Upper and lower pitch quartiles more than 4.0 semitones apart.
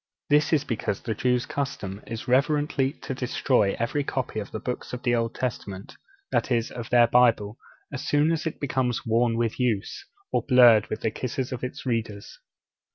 No: average, 2.7 semitones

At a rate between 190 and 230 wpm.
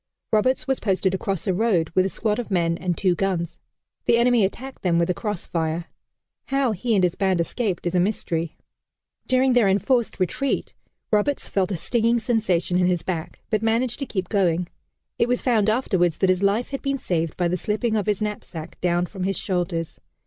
Yes: average, 200 wpm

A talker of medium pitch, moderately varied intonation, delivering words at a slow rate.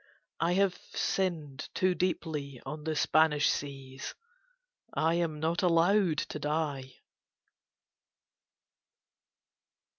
Yes: medium, 155 Hz; average, 3.1 semitones; slow, 90 wpm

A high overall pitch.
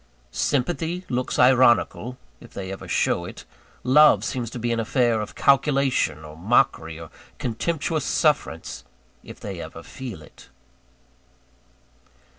No: low, 125 Hz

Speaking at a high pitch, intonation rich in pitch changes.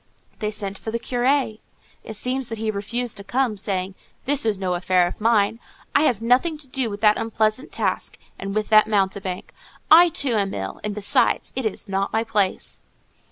No: high, 215 Hz; average, 3.6 semitones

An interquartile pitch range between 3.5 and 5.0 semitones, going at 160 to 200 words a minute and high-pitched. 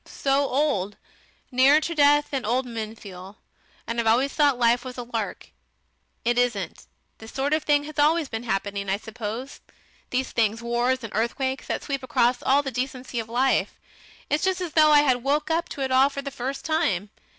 Yes: average, 3.8 semitones; average, 195 wpm; very high, 255 Hz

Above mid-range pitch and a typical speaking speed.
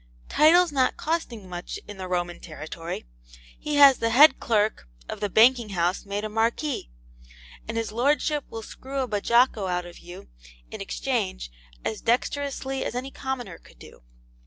Yes: high, 225 Hz; average, 165 wpm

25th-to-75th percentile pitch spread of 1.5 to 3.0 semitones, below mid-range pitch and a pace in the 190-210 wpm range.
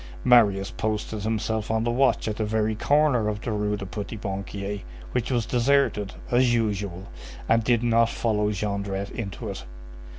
No: narrow, 2.4 semitones; low, 110 Hz; average, 165 wpm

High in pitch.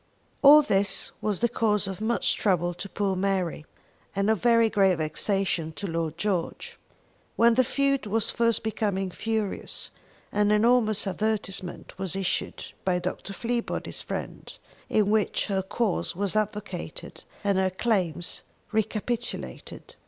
Yes: high, 205 Hz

